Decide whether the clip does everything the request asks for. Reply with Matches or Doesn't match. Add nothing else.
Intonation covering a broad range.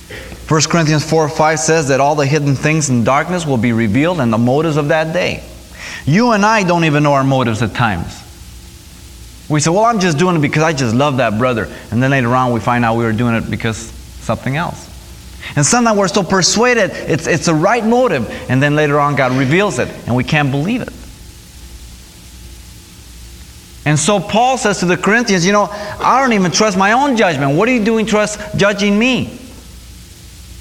Matches